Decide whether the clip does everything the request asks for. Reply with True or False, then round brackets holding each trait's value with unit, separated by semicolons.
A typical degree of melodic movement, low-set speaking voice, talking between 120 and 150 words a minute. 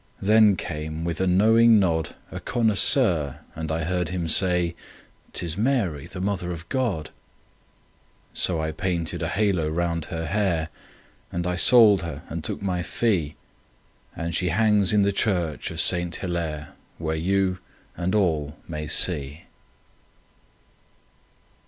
True (3.5 semitones; 85 Hz; 140 wpm)